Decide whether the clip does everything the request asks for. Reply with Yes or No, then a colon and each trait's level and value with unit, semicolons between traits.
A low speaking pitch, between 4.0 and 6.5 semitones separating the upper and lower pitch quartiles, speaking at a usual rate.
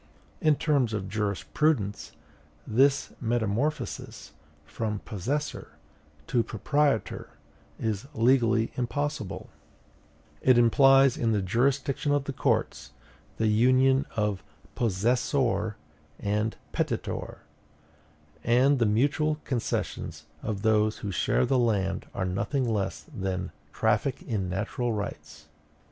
No: low, 115 Hz; average, 4.5 semitones; slow, 105 wpm